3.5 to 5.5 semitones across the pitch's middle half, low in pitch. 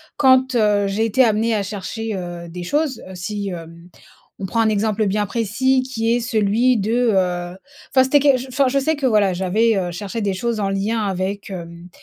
No: average, 3.9 semitones; high, 210 Hz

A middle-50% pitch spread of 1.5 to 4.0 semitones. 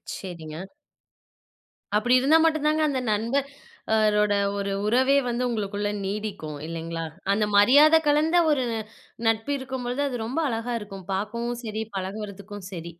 No: average, 4.5 semitones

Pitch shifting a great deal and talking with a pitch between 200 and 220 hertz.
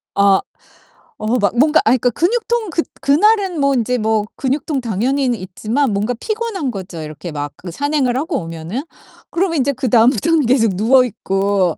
No: wide, 6.3 semitones; very high, 250 Hz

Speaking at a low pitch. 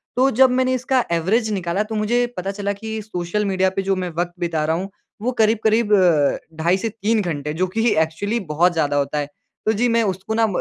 No: high, 200 Hz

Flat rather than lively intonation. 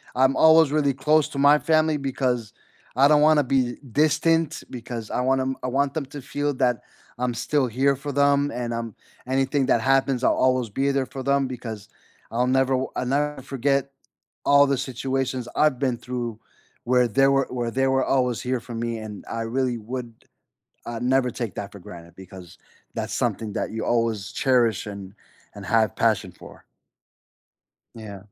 No: average, 3.0 semitones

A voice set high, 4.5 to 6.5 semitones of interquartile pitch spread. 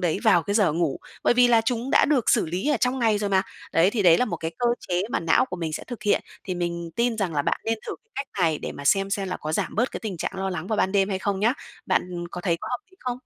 Yes: high, 195 Hz; average, 4.9 semitones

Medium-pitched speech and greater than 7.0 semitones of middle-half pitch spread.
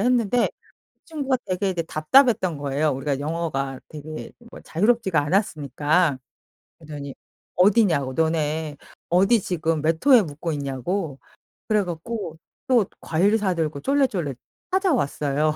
No: medium, 165 Hz; wide, 5.8 semitones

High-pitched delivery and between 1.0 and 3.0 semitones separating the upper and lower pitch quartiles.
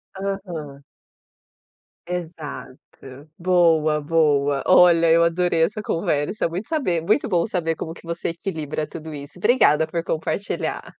No: medium, 165 Hz; average, 2.7 semitones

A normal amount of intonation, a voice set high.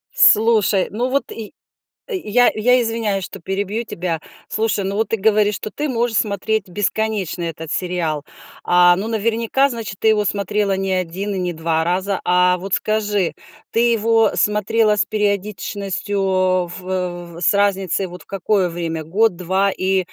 Yes: average, 3.3 semitones; high, 200 Hz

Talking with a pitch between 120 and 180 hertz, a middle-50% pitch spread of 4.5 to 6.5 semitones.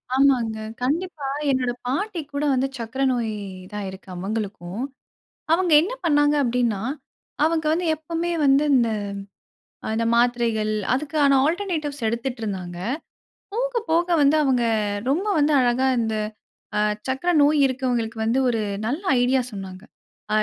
No: very high, 265 Hz; average, 5.0 semitones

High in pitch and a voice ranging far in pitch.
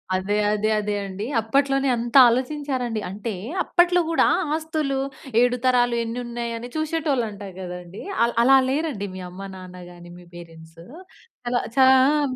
Yes: high, 240 Hz; wide, 5.8 semitones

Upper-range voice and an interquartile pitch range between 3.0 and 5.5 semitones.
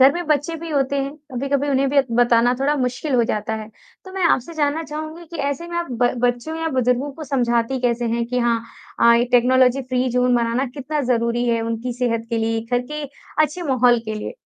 Yes: very high, 255 Hz; average, 3.5 semitones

